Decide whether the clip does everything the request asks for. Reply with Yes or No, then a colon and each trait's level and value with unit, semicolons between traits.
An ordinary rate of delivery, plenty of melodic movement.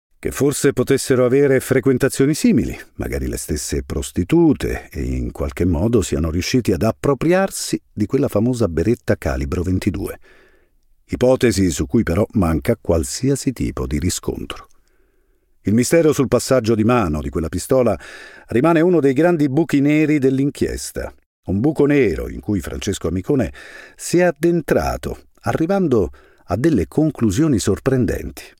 Yes: average, 135 wpm; wide, 7.4 semitones